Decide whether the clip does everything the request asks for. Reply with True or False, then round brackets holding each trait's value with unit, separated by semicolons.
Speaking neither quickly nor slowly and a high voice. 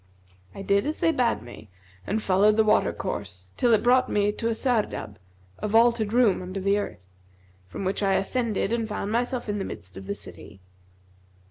True (195 wpm; 210 Hz)